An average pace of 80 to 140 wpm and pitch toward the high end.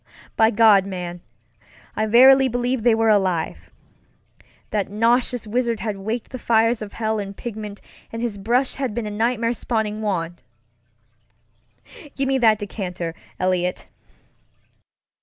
Yes: slow, 135 wpm; high, 220 Hz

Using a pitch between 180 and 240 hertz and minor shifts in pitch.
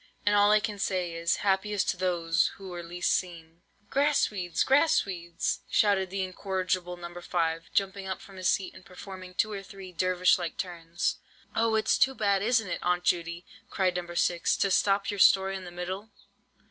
Yes: medium, 185 Hz; narrow, 2.2 semitones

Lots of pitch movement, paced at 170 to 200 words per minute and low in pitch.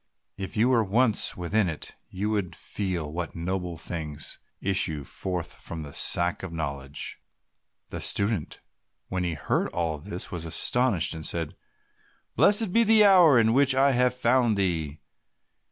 No: wide, 6.3 semitones; average, 155 wpm; very low, 95 Hz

